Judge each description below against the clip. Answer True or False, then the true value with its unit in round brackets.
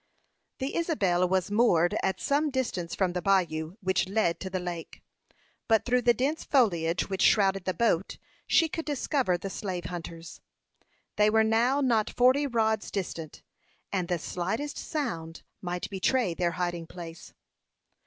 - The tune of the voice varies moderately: False (5.8 semitones)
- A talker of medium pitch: False (195 Hz)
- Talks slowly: False (155 wpm)